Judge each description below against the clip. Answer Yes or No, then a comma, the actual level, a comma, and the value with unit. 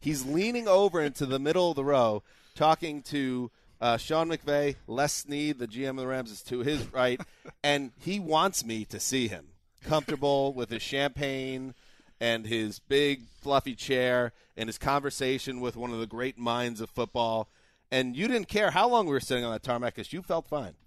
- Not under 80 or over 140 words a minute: No, average, 195 wpm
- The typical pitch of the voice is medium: No, low, 130 Hz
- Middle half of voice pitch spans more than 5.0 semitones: No, average, 3.8 semitones